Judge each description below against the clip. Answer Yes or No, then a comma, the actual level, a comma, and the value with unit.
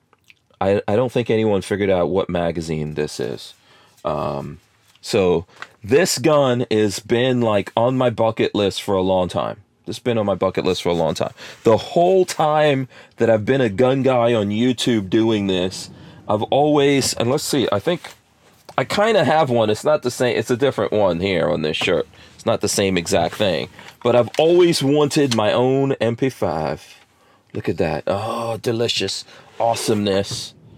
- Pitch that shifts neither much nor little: Yes, average, 4.2 semitones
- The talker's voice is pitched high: No, low, 115 Hz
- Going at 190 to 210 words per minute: No, average, 180 wpm